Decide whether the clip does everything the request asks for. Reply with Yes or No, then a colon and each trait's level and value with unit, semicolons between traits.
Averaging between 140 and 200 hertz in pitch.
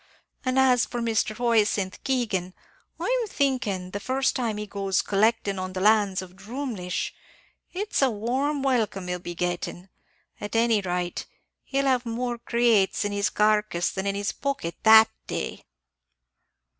No: high, 215 Hz